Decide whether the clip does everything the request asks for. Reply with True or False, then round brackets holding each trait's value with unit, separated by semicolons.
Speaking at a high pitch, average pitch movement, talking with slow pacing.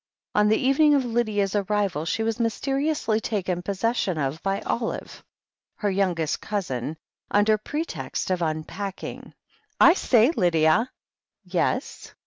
True (205 Hz; 4.6 semitones; 125 wpm)